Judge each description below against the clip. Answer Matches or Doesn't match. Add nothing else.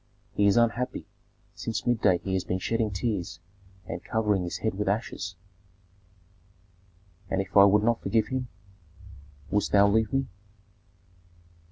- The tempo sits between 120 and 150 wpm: Matches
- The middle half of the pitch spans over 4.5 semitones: Doesn't match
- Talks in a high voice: Doesn't match